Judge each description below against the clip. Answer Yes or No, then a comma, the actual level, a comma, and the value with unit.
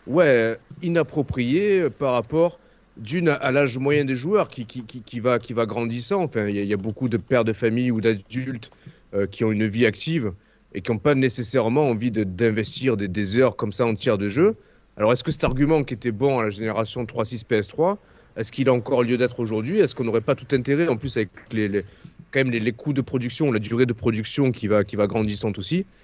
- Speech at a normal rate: No, fast, 235 wpm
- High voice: No, low, 120 Hz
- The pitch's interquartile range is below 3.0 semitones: No, average, 3.6 semitones